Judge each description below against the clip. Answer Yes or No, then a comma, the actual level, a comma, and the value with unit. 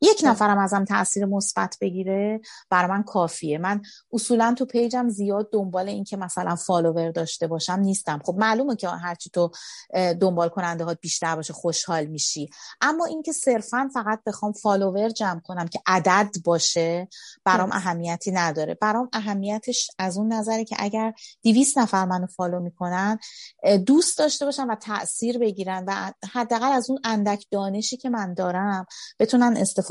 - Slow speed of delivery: No, fast, 155 wpm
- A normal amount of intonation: Yes, average, 3.9 semitones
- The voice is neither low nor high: No, high, 200 Hz